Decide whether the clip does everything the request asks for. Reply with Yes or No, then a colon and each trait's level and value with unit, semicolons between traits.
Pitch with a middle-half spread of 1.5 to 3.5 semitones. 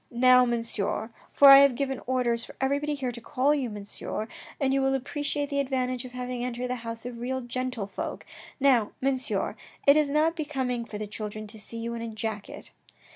Yes: average, 2.8 semitones